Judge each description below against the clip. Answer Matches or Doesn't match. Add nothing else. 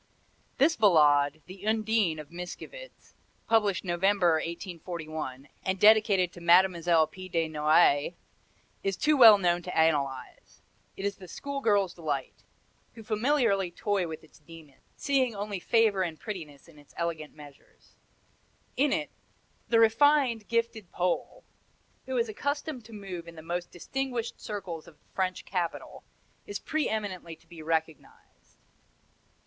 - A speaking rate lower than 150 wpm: Matches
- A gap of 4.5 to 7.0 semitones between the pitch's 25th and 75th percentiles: Matches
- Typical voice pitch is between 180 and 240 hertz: Matches